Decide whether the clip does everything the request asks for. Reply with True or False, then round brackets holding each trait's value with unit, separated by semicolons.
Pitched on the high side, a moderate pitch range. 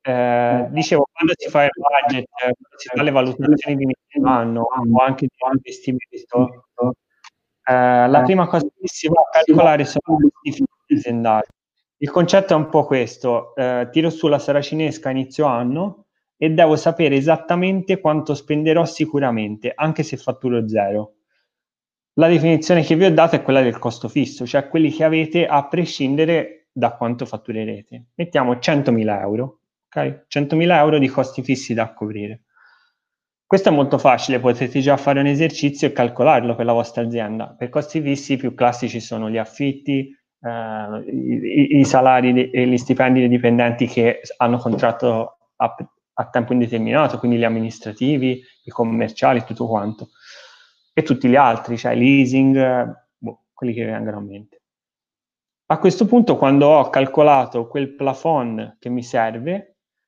False (135 Hz; 4.5 semitones)